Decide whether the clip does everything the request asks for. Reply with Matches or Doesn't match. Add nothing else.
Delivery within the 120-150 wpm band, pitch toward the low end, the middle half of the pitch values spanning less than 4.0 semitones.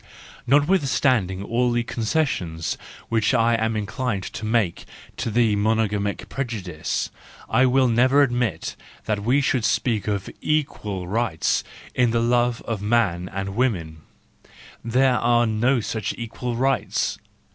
Matches